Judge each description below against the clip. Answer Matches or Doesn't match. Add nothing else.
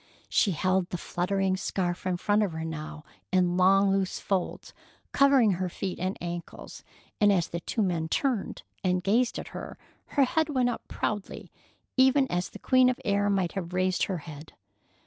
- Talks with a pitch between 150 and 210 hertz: Matches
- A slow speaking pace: Doesn't match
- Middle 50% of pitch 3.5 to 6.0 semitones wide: Doesn't match